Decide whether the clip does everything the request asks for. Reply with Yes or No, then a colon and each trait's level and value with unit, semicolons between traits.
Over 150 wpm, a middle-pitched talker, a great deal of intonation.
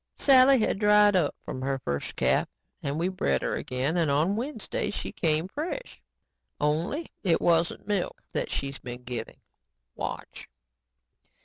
No: average, 145 wpm; medium, 170 Hz; wide, 7.0 semitones